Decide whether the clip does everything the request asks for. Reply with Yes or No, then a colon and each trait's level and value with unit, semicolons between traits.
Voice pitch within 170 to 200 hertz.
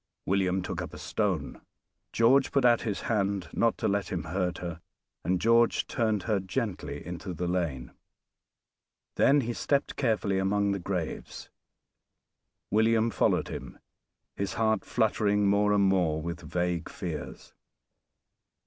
No: low, 100 Hz